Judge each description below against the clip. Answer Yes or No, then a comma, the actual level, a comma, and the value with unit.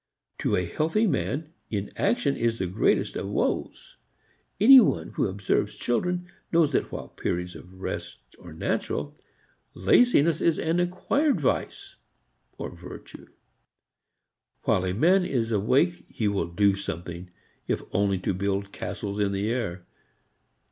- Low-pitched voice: Yes, low, 105 Hz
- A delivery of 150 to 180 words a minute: No, slow, 135 wpm